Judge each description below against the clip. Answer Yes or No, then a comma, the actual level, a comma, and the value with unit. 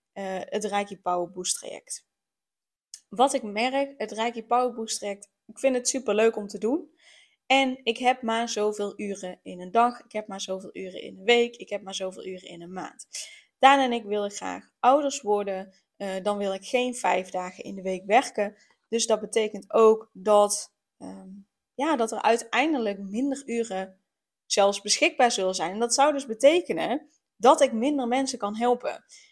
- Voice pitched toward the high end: Yes, high, 220 Hz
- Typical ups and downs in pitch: Yes, average, 4.2 semitones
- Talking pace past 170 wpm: Yes, average, 185 wpm